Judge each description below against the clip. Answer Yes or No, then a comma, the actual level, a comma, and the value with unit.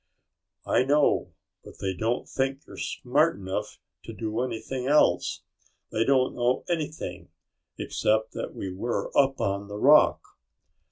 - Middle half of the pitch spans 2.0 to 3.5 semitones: No, average, 4.4 semitones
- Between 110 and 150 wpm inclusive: Yes, slow, 135 wpm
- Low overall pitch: Yes, low, 125 Hz